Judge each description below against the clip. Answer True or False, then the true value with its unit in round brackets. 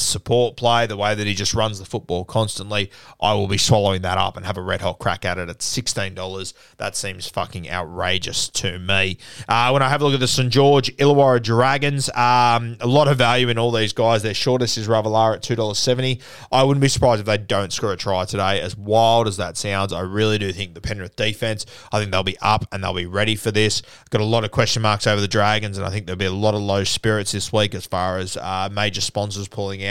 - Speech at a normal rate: False (245 wpm)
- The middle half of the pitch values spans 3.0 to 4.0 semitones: True (3.4 semitones)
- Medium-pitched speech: False (105 Hz)